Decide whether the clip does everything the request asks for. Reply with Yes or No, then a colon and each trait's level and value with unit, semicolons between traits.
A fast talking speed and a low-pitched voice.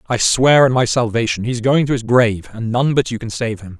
Yes: fast, 270 wpm; low, 120 Hz